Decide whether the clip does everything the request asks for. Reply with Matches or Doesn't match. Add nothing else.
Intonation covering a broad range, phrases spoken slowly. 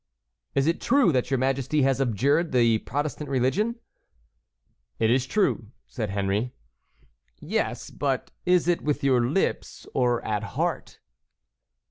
Doesn't match